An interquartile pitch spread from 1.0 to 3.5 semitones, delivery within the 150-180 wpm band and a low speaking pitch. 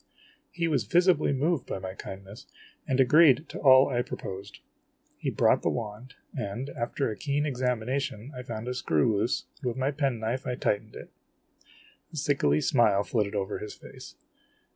No: average, 4.6 semitones; average, 170 wpm; low, 125 Hz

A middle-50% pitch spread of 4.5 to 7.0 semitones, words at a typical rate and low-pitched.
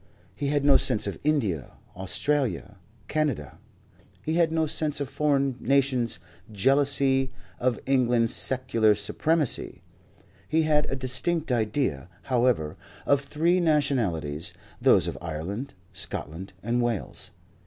No: wide, 5.5 semitones; slow, 120 wpm; low, 130 Hz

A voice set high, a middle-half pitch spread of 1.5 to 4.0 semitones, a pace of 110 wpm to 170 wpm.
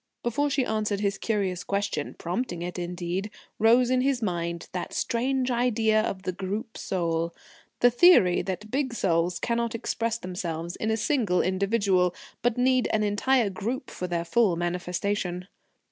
No: high, 205 Hz; average, 4.8 semitones; average, 155 wpm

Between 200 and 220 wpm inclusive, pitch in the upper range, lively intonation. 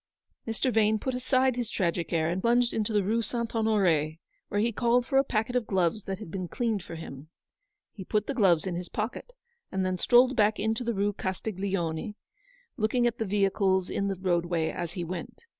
No: fast, 205 wpm; high, 205 Hz; average, 4.2 semitones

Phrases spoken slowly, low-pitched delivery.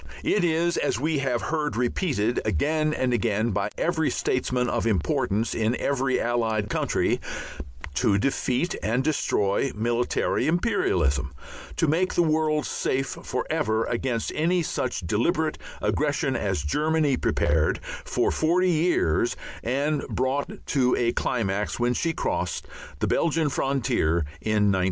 Yes: slow, 130 wpm; low, 125 Hz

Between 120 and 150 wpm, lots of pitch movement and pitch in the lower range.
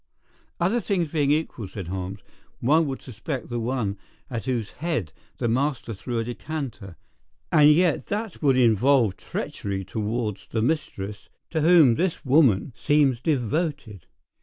Yes: average, 140 wpm; wide, 5.9 semitones; low, 130 Hz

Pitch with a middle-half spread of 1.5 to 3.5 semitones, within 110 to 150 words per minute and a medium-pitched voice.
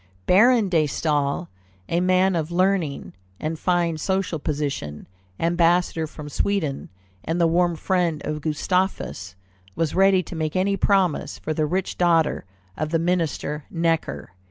Yes: average, 3.0 semitones; average, 140 wpm; medium, 170 Hz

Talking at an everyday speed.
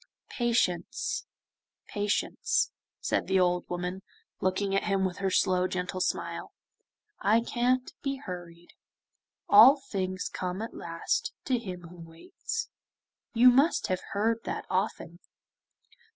No: slow, 125 wpm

